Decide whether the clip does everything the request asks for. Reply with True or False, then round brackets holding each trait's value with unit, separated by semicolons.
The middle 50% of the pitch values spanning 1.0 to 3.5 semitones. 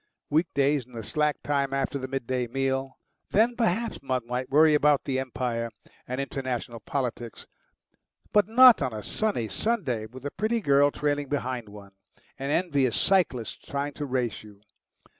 True (3.2 semitones)